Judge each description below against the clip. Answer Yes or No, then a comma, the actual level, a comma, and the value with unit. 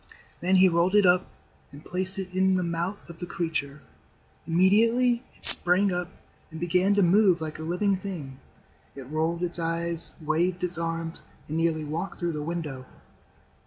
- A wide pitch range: No, narrow, 2.4 semitones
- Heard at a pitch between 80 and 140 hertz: No, medium, 175 Hz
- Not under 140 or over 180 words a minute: Yes, average, 170 wpm